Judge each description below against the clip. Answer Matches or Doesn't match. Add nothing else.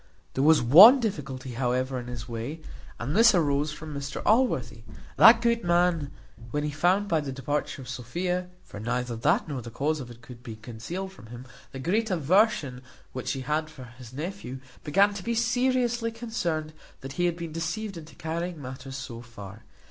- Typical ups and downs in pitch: Doesn't match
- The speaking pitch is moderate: Matches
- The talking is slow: Doesn't match